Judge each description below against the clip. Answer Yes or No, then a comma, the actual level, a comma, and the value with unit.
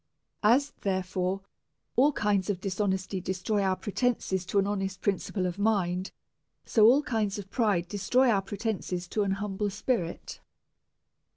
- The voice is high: Yes, high, 200 Hz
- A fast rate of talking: No, average, 145 wpm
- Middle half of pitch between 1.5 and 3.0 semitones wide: Yes, narrow, 2.4 semitones